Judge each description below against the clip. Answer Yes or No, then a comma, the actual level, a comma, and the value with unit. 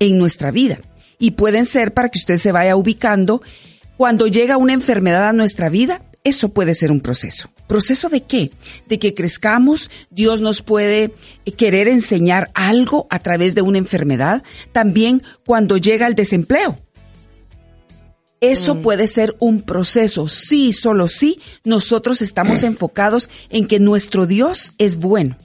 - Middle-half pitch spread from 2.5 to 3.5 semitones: No, average, 4.5 semitones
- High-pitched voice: Yes, high, 215 Hz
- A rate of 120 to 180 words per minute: Yes, average, 150 wpm